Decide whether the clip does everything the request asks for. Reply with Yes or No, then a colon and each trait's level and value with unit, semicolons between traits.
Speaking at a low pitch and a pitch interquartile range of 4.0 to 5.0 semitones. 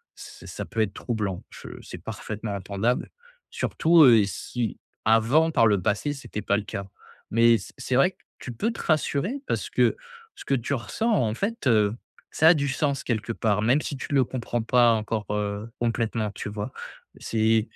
Yes: low, 115 Hz; average, 4.3 semitones